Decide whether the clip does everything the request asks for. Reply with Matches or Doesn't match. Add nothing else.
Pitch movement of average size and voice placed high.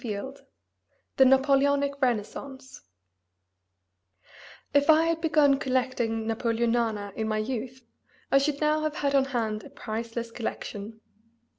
Matches